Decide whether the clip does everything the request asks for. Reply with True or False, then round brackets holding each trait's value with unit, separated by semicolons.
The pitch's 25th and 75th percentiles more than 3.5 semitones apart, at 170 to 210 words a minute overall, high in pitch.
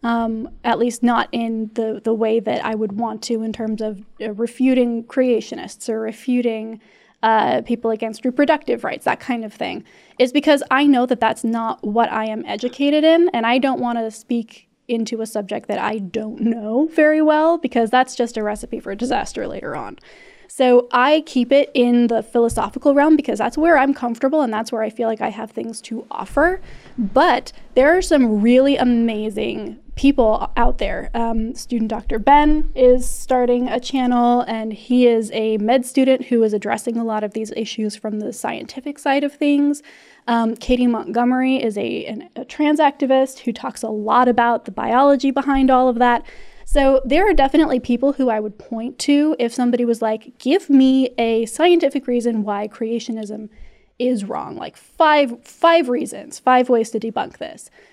False (3.1 semitones; 185 wpm; 240 Hz)